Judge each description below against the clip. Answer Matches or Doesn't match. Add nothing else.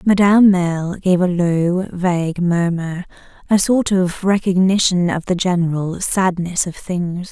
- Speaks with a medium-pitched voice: Matches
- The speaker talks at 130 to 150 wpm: Matches